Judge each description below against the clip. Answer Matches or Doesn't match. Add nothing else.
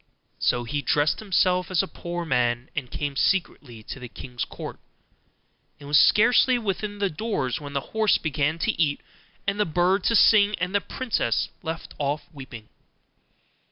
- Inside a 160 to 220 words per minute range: Matches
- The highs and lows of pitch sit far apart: Matches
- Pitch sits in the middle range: Matches